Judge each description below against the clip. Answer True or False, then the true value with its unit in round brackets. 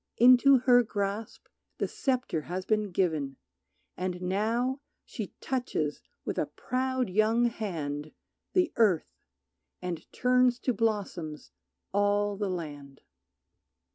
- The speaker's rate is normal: False (110 wpm)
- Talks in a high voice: True (205 Hz)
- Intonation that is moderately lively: False (5.7 semitones)